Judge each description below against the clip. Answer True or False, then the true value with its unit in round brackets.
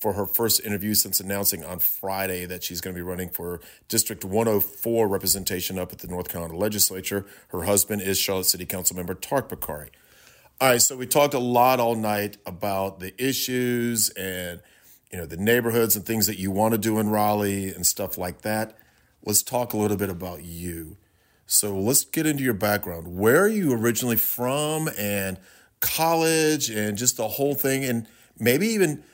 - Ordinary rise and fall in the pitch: True (4.0 semitones)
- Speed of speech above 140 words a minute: True (185 wpm)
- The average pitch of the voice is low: True (105 Hz)